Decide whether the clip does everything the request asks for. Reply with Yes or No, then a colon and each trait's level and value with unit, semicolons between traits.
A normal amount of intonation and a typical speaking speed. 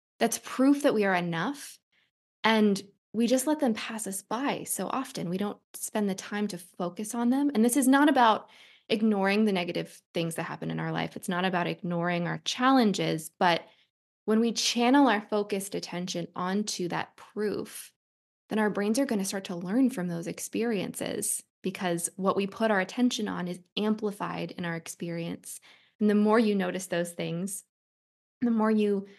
Yes: average, 4.0 semitones; average, 185 wpm